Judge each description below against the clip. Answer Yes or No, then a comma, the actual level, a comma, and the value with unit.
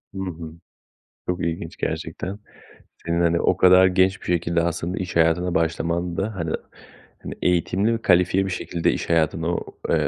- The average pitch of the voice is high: No, very low, 85 Hz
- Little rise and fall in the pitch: Yes, narrow, 1.8 semitones